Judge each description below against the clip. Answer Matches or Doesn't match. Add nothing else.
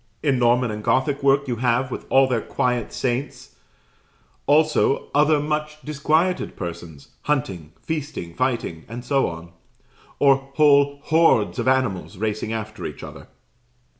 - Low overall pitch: Matches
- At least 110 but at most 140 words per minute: Matches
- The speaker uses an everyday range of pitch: Matches